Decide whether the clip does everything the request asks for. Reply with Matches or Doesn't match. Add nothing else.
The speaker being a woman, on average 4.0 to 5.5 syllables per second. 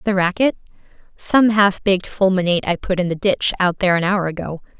Doesn't match